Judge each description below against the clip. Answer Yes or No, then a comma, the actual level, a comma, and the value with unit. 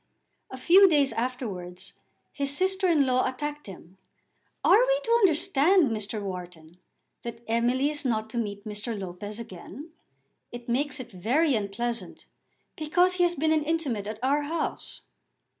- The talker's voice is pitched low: No, very high, 255 Hz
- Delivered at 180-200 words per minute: No, average, 145 wpm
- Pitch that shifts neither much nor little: No, wide, 6.7 semitones